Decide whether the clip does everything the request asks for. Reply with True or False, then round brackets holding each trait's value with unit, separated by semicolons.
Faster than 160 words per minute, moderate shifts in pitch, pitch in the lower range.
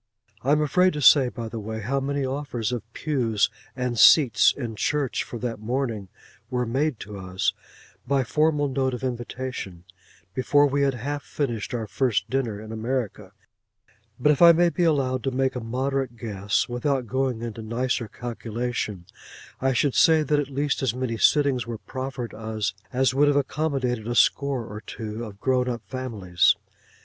True (175 wpm; 3.5 semitones; 125 Hz)